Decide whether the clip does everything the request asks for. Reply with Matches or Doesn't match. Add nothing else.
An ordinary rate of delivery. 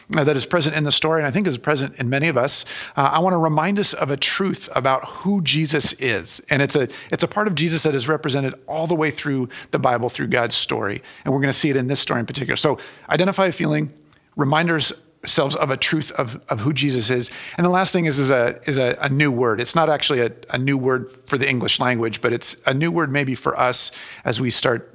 Doesn't match